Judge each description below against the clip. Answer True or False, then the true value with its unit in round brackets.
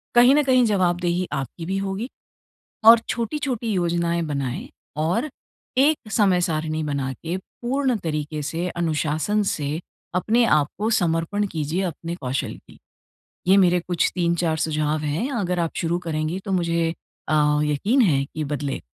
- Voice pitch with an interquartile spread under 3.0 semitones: False (4.8 semitones)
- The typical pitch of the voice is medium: True (170 Hz)